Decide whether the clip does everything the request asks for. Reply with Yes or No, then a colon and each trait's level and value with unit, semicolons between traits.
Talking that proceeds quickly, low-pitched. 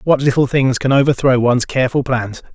No: average, 190 wpm; low, 130 Hz